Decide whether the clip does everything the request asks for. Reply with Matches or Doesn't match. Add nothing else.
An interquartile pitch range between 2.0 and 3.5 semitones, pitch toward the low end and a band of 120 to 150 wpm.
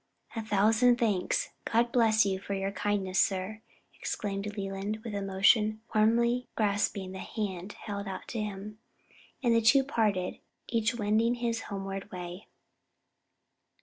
Doesn't match